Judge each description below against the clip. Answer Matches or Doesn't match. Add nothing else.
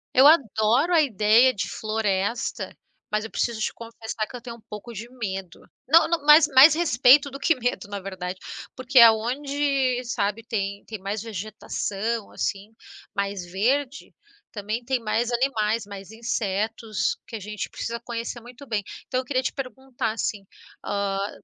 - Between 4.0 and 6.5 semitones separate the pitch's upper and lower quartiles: Doesn't match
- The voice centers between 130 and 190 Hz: Doesn't match